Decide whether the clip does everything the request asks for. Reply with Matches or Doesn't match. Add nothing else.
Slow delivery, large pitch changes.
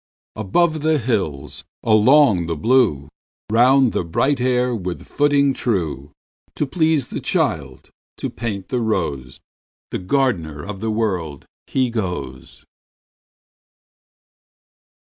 Matches